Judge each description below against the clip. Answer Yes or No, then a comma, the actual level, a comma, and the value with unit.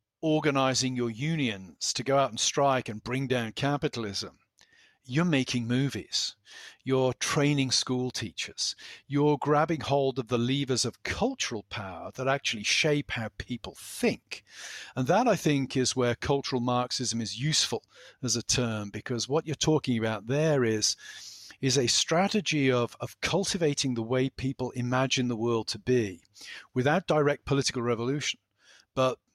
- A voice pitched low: Yes, low, 130 Hz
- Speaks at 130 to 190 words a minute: Yes, average, 150 wpm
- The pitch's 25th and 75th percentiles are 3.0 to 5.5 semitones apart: Yes, average, 3.3 semitones